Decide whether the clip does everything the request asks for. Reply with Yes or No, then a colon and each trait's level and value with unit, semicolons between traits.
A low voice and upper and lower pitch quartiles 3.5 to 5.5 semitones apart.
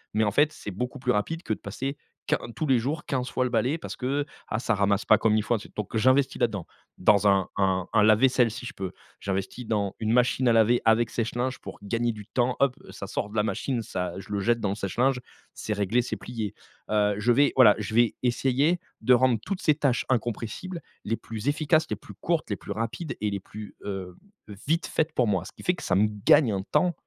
Yes: low, 115 Hz; average, 3.9 semitones